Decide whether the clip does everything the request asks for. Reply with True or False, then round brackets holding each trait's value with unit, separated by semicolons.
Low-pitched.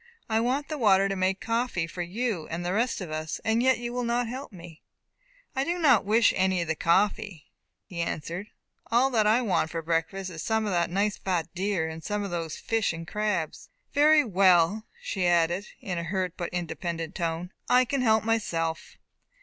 False (190 Hz)